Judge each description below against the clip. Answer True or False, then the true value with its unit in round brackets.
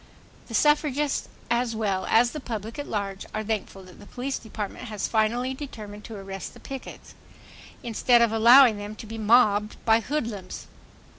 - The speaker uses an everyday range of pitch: True (3.1 semitones)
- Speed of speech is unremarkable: True (165 wpm)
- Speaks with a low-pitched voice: False (225 Hz)